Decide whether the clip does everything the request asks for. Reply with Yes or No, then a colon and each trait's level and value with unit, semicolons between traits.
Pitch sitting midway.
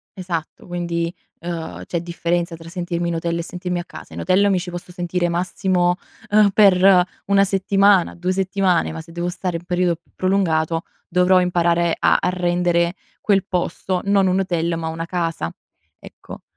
Yes: medium, 175 Hz